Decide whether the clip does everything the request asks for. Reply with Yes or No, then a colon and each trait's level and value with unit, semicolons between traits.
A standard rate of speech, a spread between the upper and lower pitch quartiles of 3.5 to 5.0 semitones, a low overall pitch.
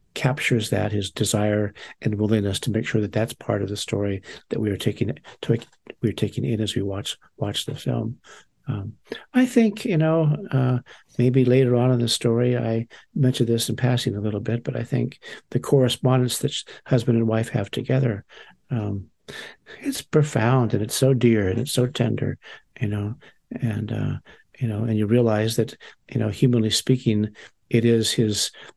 No: average, 185 wpm; average, 2.9 semitones; low, 115 Hz